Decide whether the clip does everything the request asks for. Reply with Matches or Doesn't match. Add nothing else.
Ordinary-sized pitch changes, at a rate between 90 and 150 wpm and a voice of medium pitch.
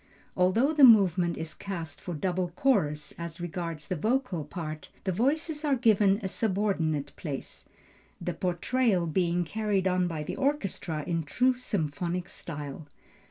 Matches